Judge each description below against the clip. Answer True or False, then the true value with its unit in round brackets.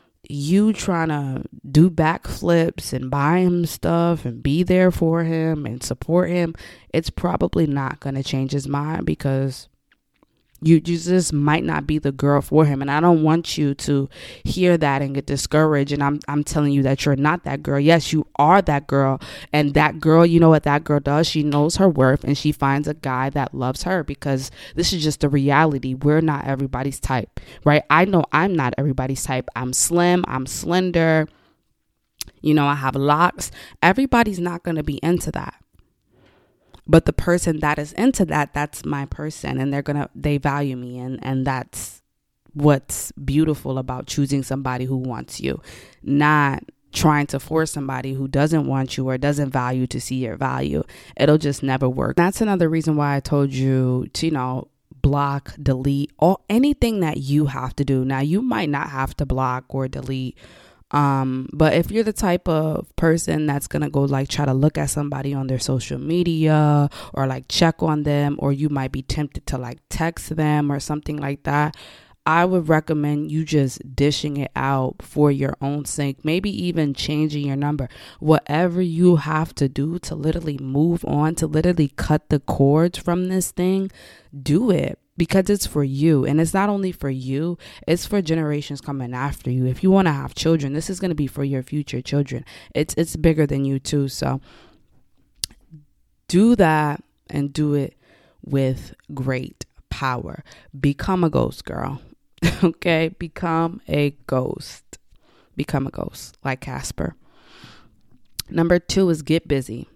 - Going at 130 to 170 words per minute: False (180 wpm)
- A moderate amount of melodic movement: True (3.1 semitones)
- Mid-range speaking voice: True (145 Hz)